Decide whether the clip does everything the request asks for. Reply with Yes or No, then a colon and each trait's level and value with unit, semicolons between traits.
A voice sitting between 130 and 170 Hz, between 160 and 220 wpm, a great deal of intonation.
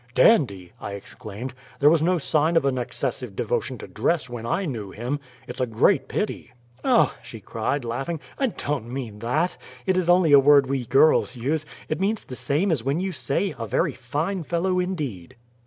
Yes: low, 135 Hz; average, 190 wpm; wide, 5.7 semitones